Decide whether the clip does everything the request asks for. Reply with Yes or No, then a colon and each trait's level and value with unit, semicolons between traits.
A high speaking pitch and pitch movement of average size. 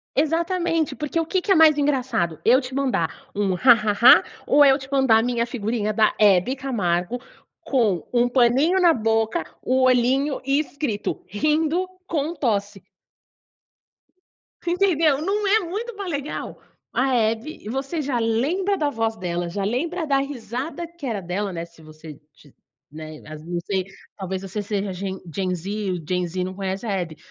No: high, 240 Hz; wide, 7.3 semitones